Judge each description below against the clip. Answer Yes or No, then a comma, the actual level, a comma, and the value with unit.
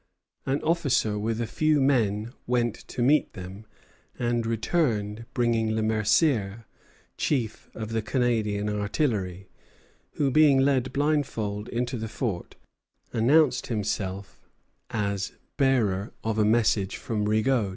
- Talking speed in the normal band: No, slow, 120 wpm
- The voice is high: No, low, 115 Hz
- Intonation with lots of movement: No, average, 3.9 semitones